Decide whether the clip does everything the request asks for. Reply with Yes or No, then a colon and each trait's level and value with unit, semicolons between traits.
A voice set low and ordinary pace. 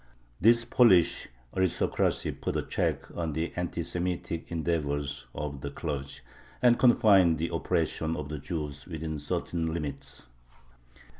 No: very low, 80 Hz; slow, 130 wpm